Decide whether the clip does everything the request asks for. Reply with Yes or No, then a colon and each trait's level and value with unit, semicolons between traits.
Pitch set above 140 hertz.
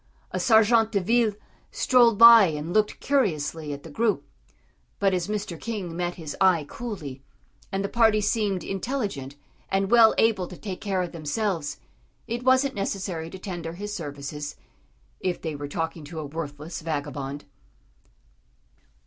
Yes: medium, 185 Hz